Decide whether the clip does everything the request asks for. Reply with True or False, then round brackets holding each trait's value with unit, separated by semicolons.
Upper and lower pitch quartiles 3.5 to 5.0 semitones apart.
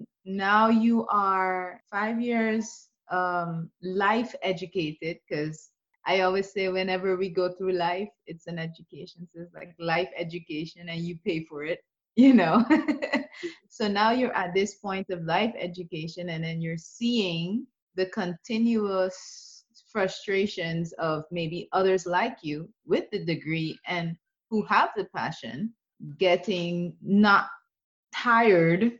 True (4.3 semitones)